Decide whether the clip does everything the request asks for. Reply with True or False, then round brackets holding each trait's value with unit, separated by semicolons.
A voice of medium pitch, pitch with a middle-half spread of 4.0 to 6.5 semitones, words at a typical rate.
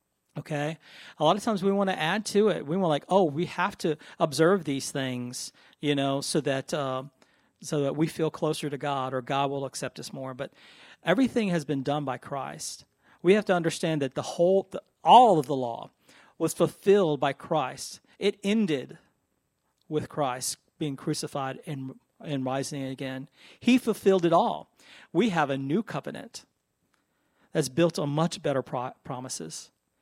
True (155 Hz; 4.6 semitones; 175 wpm)